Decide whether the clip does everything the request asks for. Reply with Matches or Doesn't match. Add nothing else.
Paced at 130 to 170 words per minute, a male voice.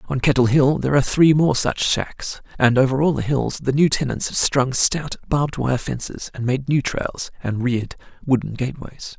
Doesn't match